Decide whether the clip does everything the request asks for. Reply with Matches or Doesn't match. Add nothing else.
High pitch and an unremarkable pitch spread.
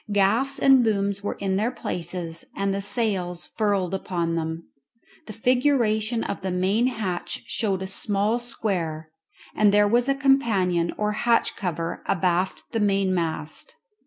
Matches